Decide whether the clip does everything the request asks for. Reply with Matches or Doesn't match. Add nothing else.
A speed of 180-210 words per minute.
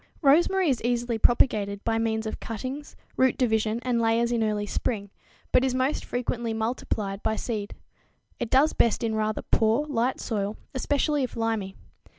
Doesn't match